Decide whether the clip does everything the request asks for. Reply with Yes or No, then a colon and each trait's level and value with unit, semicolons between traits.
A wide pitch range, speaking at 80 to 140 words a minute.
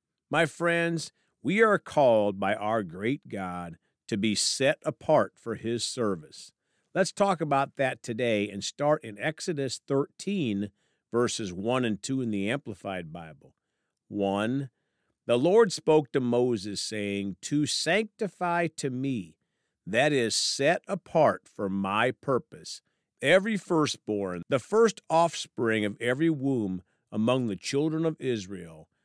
Yes: wide, 7.7 semitones; slow, 135 wpm